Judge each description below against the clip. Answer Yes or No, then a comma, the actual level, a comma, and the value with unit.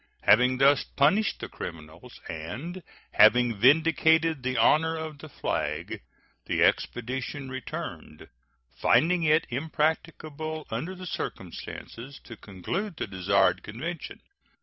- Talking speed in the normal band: No, slow, 110 wpm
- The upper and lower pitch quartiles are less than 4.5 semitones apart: No, average, 5.0 semitones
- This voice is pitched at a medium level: Yes, medium, 145 Hz